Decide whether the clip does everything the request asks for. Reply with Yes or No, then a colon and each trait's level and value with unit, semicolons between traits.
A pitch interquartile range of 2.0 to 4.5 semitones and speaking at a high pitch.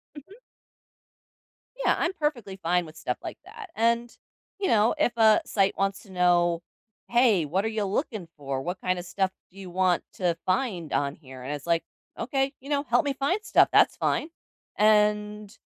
No: wide, 5.4 semitones; high, 200 Hz